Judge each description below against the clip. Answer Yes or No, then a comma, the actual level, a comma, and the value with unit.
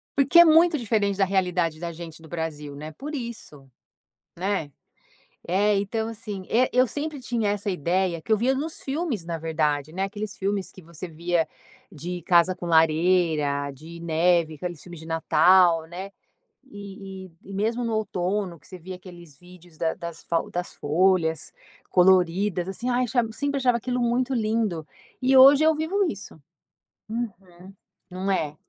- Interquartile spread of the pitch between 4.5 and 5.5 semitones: Yes, average, 5.0 semitones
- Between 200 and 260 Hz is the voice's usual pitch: No, medium, 185 Hz